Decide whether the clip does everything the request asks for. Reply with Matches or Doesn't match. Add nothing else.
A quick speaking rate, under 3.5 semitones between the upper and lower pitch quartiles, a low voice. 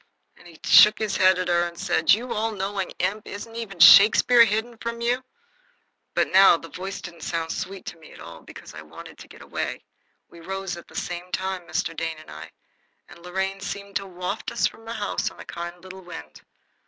Doesn't match